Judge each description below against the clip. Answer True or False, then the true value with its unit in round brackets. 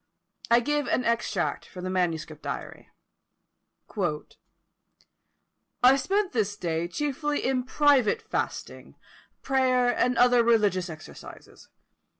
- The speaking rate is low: True (105 wpm)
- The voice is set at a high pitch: True (245 Hz)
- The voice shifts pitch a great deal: True (6.5 semitones)